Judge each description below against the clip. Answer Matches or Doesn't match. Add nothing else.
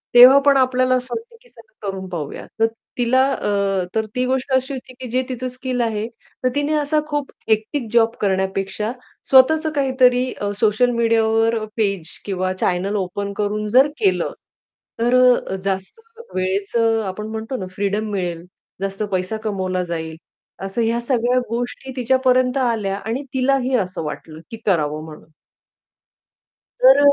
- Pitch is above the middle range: Matches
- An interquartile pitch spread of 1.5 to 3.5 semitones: Doesn't match